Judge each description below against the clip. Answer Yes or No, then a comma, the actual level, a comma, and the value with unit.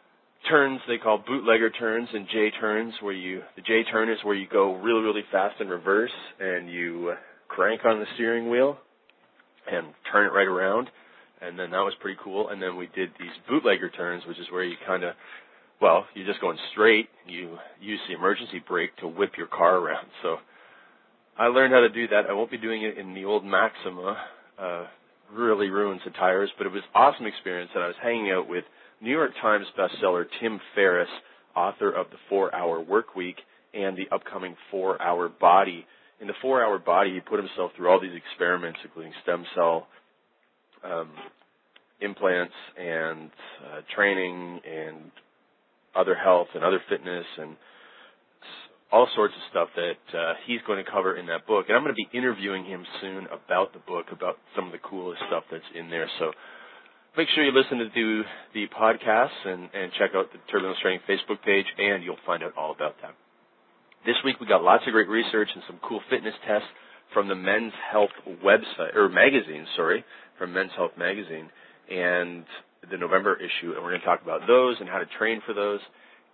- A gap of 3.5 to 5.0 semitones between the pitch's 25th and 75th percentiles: Yes, average, 4.0 semitones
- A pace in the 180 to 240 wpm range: Yes, average, 190 wpm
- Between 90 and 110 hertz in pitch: Yes, low, 100 Hz